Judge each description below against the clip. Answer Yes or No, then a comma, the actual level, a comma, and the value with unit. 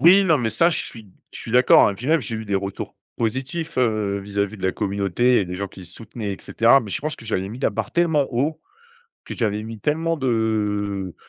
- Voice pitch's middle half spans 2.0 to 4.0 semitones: No, average, 5.0 semitones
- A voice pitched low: Yes, low, 110 Hz